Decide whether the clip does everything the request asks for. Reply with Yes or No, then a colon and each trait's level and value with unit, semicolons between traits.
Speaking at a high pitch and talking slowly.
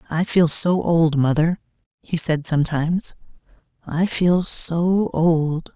No: medium, 165 Hz; slow, 125 wpm